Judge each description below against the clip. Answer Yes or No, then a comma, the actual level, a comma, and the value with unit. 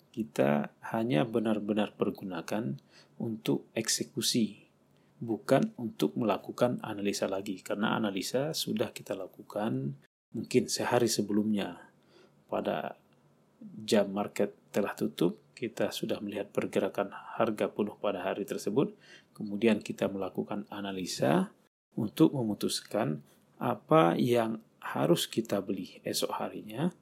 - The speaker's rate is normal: Yes, average, 100 wpm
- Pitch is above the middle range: No, low, 105 Hz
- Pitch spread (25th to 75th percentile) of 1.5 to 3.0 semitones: Yes, narrow, 2.6 semitones